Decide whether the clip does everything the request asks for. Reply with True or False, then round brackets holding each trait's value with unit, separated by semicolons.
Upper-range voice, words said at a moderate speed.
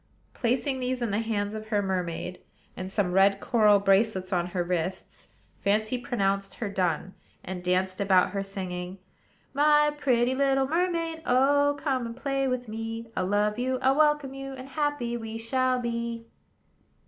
True (230 Hz; 160 wpm)